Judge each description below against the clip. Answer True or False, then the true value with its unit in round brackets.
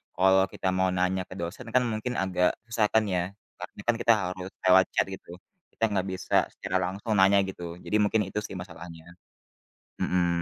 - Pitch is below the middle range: True (95 Hz)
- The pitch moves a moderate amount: False (2.2 semitones)